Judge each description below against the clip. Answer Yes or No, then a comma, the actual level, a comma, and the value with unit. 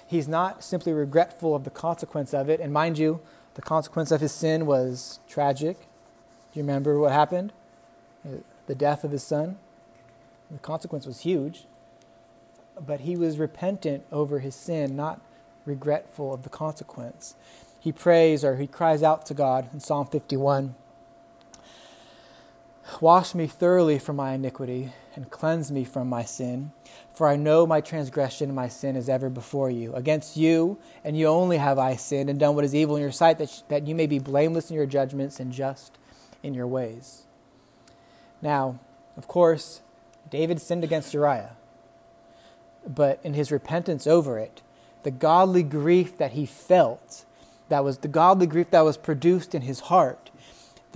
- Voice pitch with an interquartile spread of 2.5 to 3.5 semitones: Yes, average, 2.9 semitones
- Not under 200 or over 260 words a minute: No, average, 165 wpm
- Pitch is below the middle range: No, medium, 145 Hz